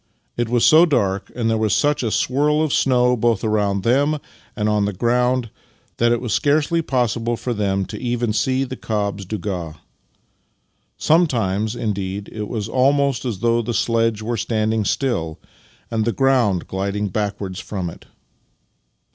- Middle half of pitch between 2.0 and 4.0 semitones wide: Yes, average, 3.5 semitones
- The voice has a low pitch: Yes, low, 115 Hz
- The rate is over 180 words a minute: No, average, 160 wpm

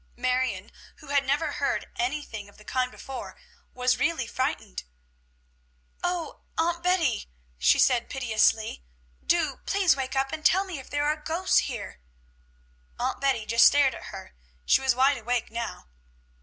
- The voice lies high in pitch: Yes, very high, 265 Hz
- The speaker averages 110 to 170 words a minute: Yes, average, 155 wpm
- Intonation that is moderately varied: Yes, average, 4.6 semitones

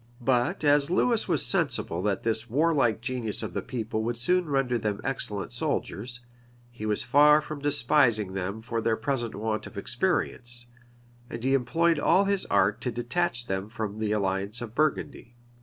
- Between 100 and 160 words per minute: No, average, 170 wpm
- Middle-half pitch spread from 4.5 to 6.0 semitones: Yes, average, 4.9 semitones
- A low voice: Yes, low, 120 Hz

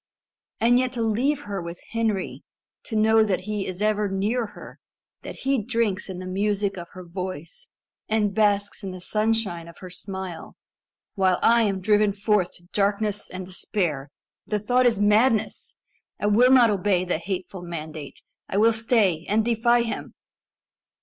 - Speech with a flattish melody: No, average, 3.2 semitones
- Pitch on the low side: No, high, 205 Hz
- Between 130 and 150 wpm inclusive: No, average, 165 wpm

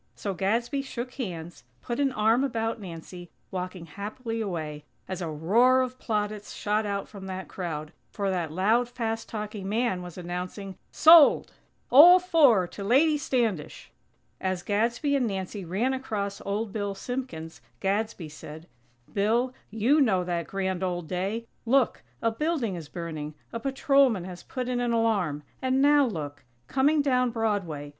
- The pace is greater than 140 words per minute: Yes, average, 155 wpm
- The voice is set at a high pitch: Yes, high, 210 Hz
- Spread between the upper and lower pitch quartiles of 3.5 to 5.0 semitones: No, wide, 5.4 semitones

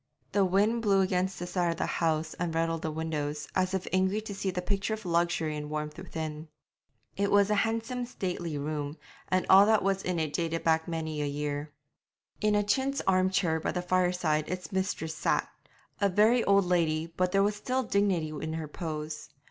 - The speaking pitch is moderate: Yes, medium, 180 Hz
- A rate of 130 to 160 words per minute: No, average, 200 wpm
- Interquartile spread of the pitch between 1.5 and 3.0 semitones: No, average, 3.8 semitones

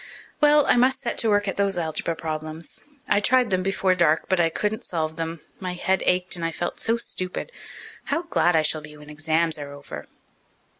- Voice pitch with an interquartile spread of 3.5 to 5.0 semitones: Yes, average, 4.2 semitones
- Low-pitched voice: No, medium, 175 Hz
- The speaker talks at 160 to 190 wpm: No, fast, 205 wpm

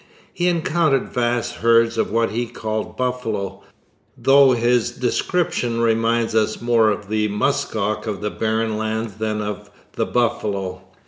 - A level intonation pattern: Yes, narrow, 2.1 semitones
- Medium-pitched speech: No, low, 115 Hz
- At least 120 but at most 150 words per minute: Yes, average, 145 wpm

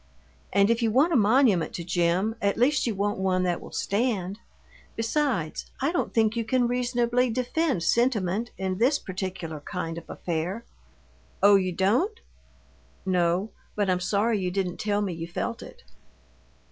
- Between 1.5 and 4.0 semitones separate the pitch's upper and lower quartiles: No, average, 4.6 semitones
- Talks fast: No, average, 160 wpm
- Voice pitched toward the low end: No, high, 205 Hz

